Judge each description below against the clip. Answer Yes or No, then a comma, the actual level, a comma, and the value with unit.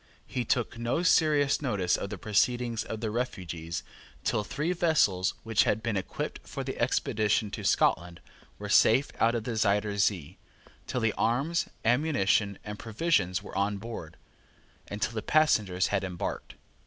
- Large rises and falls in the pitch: No, average, 3.8 semitones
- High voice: No, low, 110 Hz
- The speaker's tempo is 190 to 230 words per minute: No, average, 160 wpm